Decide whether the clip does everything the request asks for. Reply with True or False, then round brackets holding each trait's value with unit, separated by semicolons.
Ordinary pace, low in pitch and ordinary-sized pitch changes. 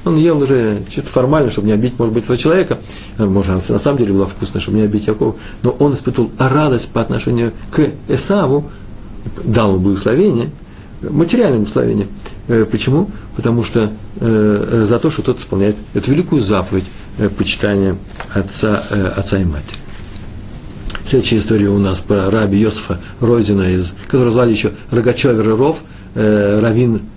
True (145 wpm; 110 Hz; 3.3 semitones)